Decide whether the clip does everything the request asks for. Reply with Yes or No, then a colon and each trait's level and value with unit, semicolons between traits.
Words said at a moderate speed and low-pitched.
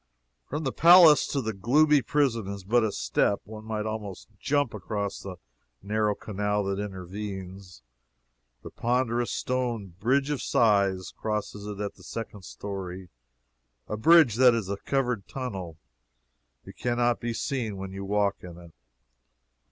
Yes: average, 150 wpm; low, 105 Hz